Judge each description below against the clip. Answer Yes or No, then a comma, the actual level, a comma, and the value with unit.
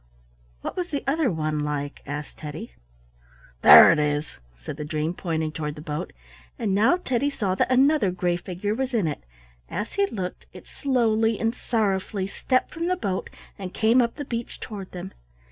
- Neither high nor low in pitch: No, high, 195 Hz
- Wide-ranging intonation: Yes, wide, 7.9 semitones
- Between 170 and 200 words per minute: Yes, average, 180 wpm